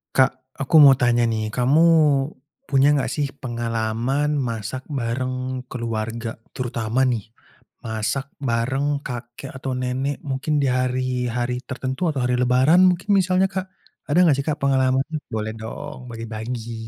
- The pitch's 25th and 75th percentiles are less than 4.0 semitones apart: Yes, average, 2.8 semitones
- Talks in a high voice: No, low, 125 Hz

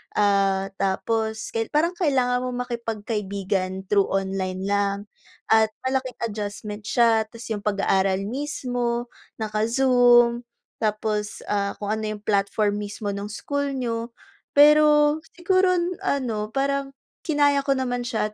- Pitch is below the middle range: No, high, 220 Hz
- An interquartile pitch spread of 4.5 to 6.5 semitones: No, average, 3.9 semitones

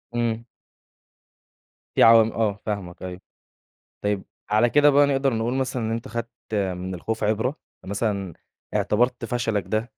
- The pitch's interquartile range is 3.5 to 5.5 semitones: No, average, 2.9 semitones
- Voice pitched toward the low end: Yes, low, 110 Hz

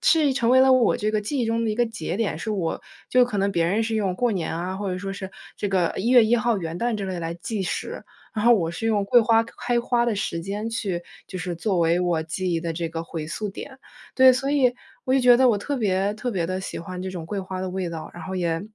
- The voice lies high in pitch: Yes, high, 200 Hz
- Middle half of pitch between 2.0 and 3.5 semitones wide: No, average, 4.8 semitones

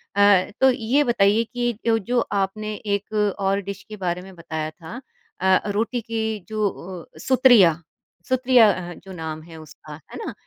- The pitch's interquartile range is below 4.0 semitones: No, average, 4.3 semitones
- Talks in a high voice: Yes, high, 205 Hz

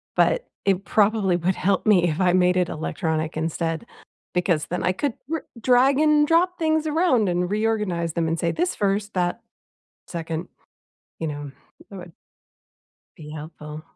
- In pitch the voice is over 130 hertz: Yes, medium, 185 Hz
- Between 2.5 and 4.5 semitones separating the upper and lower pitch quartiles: No, average, 5.2 semitones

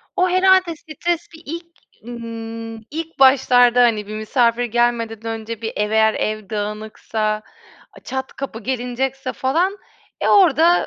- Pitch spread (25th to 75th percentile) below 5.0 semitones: No, wide, 5.6 semitones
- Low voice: No, high, 240 Hz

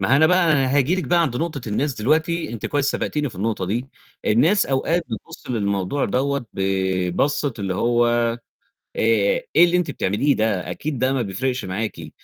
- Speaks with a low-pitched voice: Yes, low, 125 Hz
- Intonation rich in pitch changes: Yes, wide, 5.9 semitones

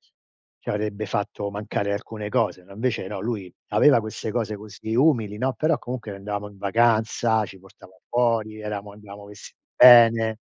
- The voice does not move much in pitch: Yes, narrow, 2.0 semitones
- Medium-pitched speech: No, low, 105 Hz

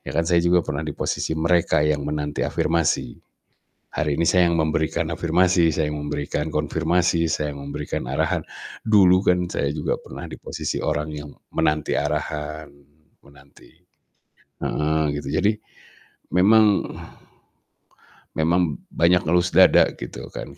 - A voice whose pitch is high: No, very low, 80 Hz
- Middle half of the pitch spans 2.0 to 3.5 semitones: Yes, average, 2.7 semitones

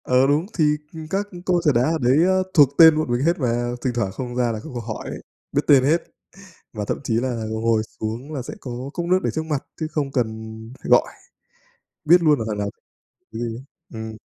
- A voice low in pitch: Yes, low, 130 Hz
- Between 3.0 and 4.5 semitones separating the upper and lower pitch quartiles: No, average, 5.2 semitones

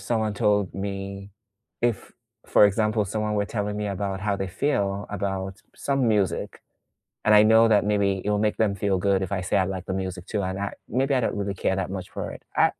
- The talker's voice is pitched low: Yes, low, 100 Hz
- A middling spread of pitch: No, narrow, 1.7 semitones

